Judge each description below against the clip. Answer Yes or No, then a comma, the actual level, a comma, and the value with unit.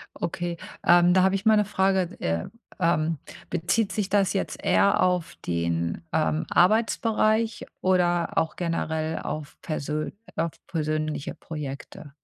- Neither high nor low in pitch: Yes, medium, 170 Hz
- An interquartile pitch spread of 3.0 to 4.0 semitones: Yes, average, 3.6 semitones